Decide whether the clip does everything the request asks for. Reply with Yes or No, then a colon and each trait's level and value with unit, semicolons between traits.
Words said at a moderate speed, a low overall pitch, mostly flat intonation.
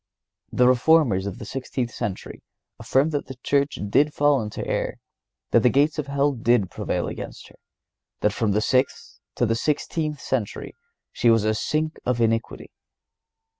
No: average, 165 wpm; low, 125 Hz; average, 4.2 semitones